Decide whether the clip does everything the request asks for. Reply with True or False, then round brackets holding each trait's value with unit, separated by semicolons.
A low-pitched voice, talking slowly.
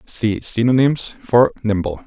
True (115 Hz; 115 wpm)